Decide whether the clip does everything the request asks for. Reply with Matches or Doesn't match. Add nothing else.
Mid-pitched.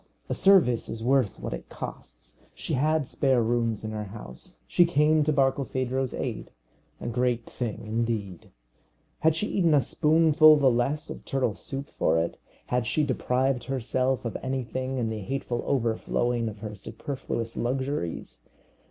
Doesn't match